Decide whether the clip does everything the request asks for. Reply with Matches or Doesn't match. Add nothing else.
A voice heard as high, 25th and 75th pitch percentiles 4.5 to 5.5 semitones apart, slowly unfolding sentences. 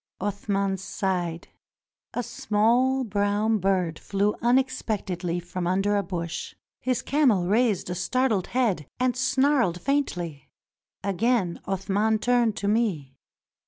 Matches